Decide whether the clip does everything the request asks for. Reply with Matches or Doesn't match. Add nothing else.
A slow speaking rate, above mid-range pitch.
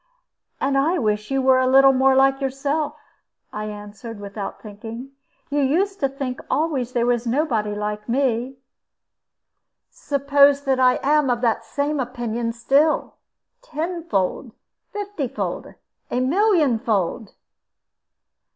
Matches